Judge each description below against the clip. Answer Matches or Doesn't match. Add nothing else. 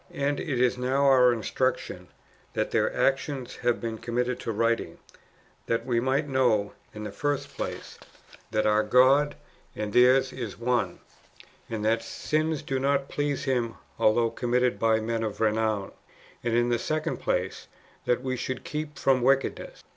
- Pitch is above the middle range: Doesn't match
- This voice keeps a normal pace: Matches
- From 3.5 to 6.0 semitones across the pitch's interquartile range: Doesn't match